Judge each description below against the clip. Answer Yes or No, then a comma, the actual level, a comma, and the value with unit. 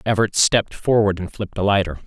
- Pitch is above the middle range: No, low, 100 Hz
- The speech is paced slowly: No, fast, 205 wpm